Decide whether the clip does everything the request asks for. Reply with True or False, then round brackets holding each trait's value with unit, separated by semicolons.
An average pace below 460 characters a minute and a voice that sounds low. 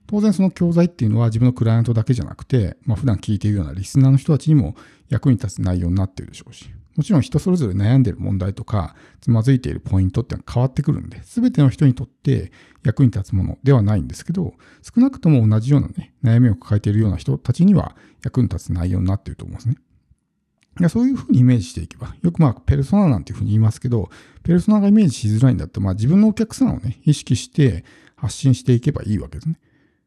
False (525 characters per minute; 125 Hz)